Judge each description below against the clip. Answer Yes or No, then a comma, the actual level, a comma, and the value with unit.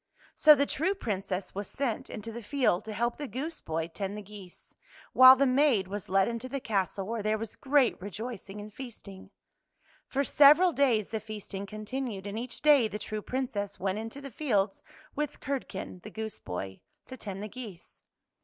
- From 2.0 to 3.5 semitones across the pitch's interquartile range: No, average, 4.8 semitones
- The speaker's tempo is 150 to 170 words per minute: No, average, 190 wpm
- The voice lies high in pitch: Yes, high, 220 Hz